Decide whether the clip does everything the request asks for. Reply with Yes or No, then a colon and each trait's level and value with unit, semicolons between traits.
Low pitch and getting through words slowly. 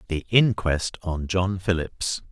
Yes: very low, 90 Hz; slow, 130 wpm